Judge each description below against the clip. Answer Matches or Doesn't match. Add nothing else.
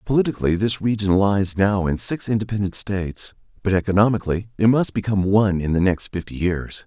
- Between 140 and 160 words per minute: Doesn't match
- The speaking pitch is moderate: Doesn't match